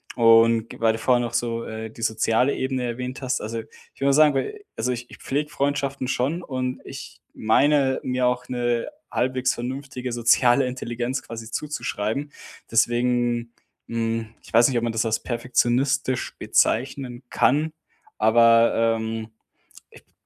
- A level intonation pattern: Yes, narrow, 2.2 semitones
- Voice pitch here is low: Yes, low, 120 Hz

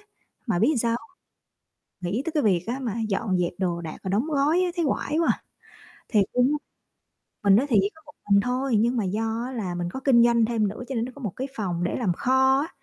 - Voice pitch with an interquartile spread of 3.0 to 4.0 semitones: No, average, 5.0 semitones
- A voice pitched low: No, high, 235 Hz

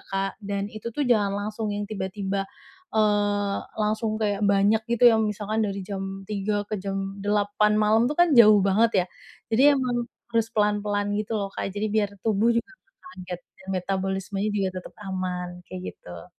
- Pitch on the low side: No, high, 205 Hz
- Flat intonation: Yes, narrow, 1.9 semitones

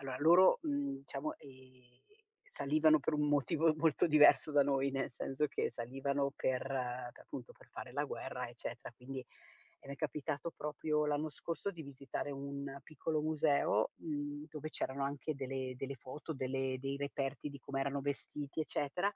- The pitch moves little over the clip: Yes, narrow, 2.2 semitones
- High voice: No, medium, 140 Hz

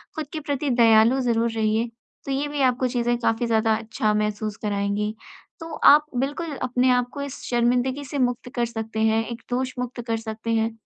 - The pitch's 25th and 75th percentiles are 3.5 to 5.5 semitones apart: No, average, 2.8 semitones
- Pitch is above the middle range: Yes, high, 235 Hz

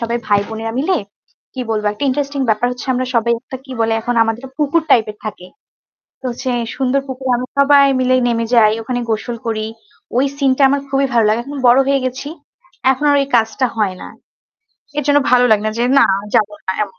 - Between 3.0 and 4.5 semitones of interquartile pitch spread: Yes, average, 3.5 semitones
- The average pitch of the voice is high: Yes, high, 245 Hz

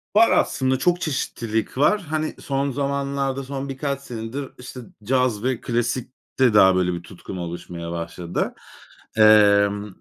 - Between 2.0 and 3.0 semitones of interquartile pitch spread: No, average, 5.2 semitones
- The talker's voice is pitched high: No, low, 125 Hz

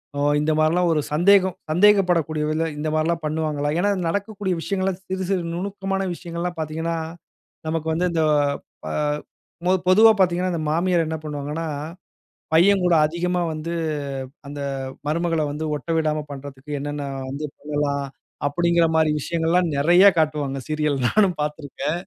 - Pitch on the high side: No, medium, 165 Hz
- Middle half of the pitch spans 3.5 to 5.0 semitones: No, average, 3.0 semitones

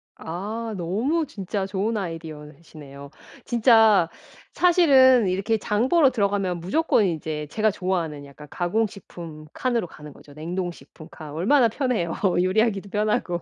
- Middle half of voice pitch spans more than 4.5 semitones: Yes, average, 5.3 semitones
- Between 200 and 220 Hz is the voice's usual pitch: No, high, 190 Hz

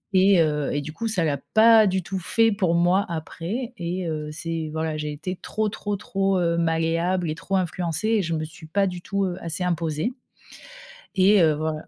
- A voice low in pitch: No, medium, 175 Hz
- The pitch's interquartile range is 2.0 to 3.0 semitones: No, average, 3.4 semitones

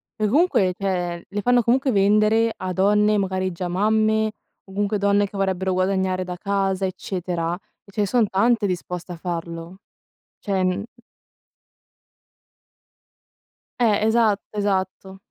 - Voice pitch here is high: Yes, high, 195 Hz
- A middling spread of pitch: No, narrow, 2.3 semitones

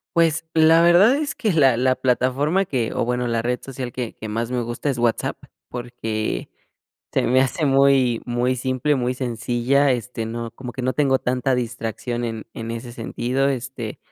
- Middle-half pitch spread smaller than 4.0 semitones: Yes, narrow, 2.5 semitones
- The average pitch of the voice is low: Yes, low, 125 Hz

